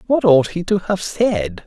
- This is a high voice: No, medium, 175 Hz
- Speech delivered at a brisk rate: Yes, fast, 215 wpm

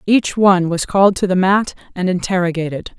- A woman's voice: Yes, female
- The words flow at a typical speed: Yes, average, 180 wpm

